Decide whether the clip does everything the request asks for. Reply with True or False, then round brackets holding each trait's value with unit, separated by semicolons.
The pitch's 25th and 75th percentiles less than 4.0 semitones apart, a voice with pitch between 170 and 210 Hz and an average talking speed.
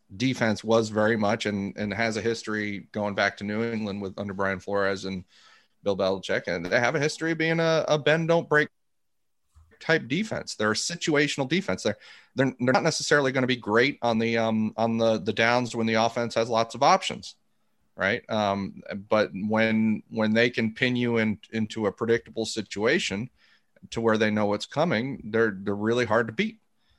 False (2.9 semitones; 110 Hz; 195 wpm)